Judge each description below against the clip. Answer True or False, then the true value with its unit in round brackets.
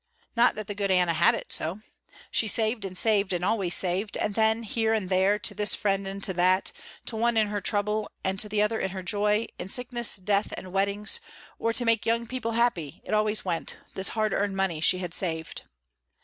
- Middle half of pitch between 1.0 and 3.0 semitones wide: True (2.7 semitones)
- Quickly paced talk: True (220 wpm)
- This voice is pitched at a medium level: False (205 Hz)